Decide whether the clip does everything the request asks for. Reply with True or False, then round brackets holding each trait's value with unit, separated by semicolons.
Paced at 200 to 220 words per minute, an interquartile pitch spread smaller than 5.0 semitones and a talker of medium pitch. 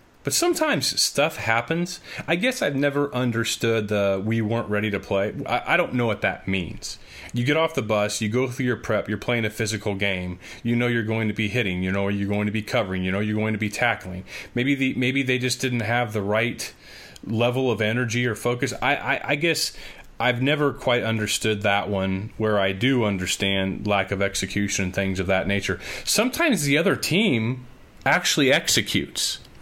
False (205 wpm; 4.1 semitones; 110 Hz)